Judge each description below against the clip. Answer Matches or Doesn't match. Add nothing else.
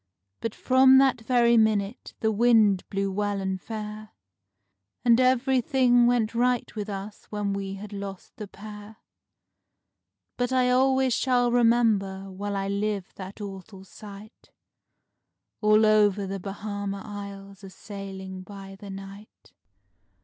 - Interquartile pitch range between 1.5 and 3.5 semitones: Matches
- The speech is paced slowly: Matches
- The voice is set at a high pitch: Matches